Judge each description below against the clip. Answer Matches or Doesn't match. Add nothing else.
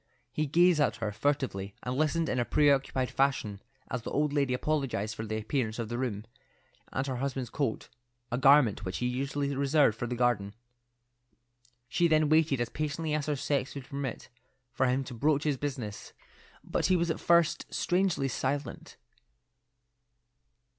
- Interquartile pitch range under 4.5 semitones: Matches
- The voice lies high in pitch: Doesn't match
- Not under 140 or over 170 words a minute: Matches